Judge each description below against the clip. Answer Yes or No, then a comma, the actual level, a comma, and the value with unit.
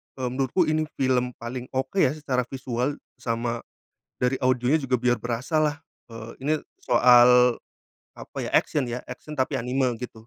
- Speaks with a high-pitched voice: No, low, 125 Hz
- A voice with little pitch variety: Yes, narrow, 2.0 semitones